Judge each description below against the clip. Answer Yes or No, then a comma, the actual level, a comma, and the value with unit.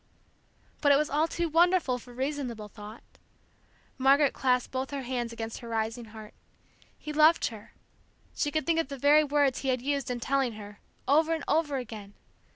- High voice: Yes, very high, 265 Hz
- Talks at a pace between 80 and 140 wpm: No, average, 180 wpm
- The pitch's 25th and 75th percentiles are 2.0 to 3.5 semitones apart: No, average, 4.1 semitones